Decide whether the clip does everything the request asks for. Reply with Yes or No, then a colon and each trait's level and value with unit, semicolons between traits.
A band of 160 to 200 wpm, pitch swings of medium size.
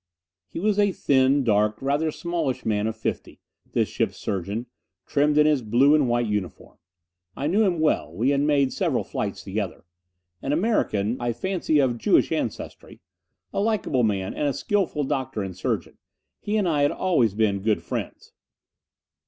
No: average, 170 wpm; wide, 6.0 semitones